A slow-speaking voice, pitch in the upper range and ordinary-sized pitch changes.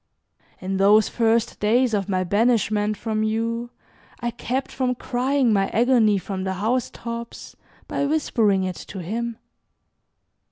Yes: slow, 130 wpm; high, 225 Hz; average, 3.0 semitones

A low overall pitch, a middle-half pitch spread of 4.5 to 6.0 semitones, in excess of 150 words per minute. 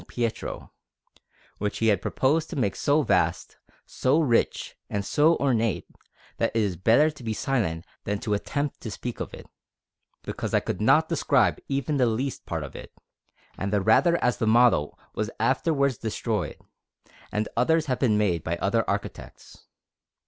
Yes: low, 115 Hz; average, 5.1 semitones; average, 165 wpm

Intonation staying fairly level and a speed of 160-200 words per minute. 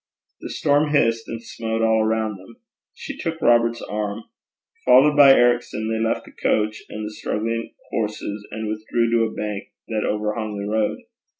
Yes: narrow, 1.6 semitones; average, 170 wpm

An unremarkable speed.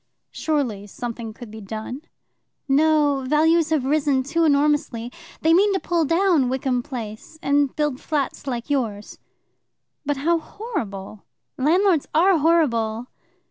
No: slow, 130 wpm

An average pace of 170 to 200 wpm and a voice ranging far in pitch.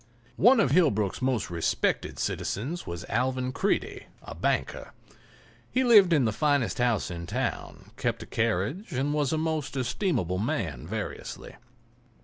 No: average, 140 wpm; wide, 7.1 semitones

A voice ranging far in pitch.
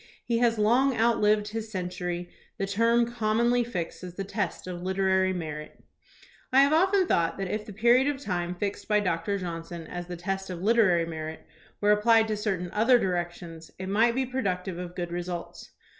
No: average, 4.5 semitones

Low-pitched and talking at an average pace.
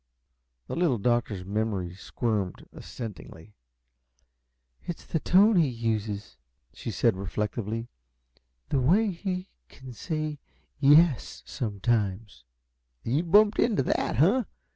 No: low, 120 Hz; slow, 110 wpm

